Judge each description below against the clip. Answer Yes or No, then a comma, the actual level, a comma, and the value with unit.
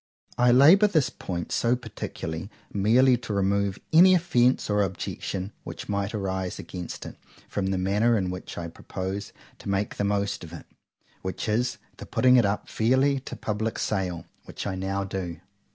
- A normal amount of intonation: Yes, average, 4.2 semitones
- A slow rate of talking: No, average, 170 wpm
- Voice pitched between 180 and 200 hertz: No, low, 100 Hz